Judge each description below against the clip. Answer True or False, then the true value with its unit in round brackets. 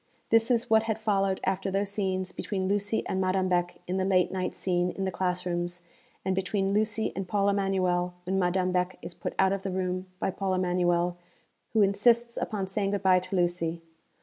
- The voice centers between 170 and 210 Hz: True (190 Hz)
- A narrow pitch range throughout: True (1.7 semitones)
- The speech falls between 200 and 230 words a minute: True (205 wpm)